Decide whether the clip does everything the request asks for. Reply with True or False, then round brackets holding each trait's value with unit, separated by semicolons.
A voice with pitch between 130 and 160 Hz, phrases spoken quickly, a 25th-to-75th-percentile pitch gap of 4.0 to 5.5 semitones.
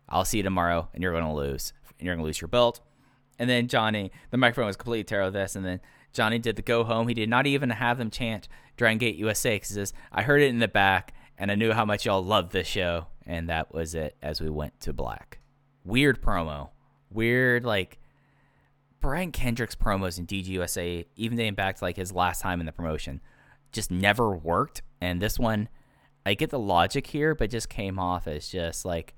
False (105 Hz; 215 wpm; 5.1 semitones)